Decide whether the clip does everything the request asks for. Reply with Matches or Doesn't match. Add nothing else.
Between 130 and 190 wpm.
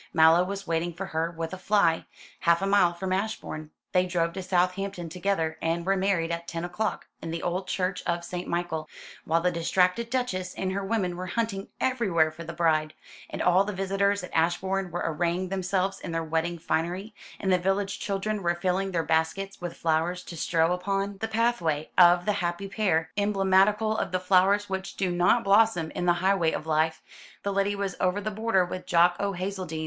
Doesn't match